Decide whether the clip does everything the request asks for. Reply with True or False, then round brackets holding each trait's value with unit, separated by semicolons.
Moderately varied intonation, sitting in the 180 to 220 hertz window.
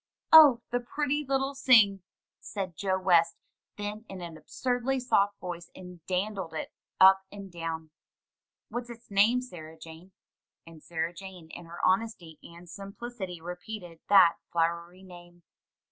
True (4.4 semitones; 190 Hz)